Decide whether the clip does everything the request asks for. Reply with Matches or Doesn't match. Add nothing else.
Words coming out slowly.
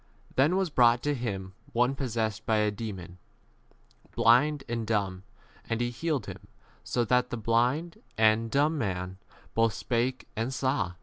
Doesn't match